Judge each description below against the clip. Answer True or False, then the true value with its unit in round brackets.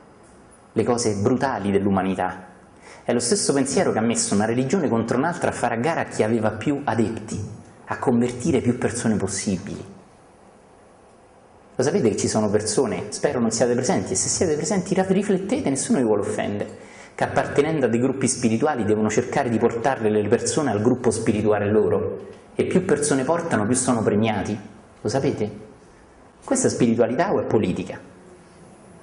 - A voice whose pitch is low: True (115 Hz)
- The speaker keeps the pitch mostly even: False (3.7 semitones)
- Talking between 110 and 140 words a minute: False (165 wpm)